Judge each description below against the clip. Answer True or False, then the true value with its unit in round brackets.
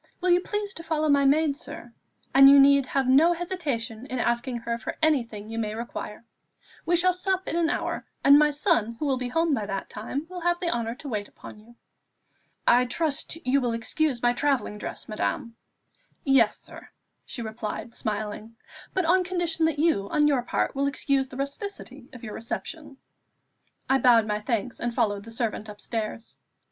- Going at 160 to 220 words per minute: True (190 wpm)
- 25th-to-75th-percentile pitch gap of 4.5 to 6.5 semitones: True (5.5 semitones)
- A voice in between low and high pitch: False (265 Hz)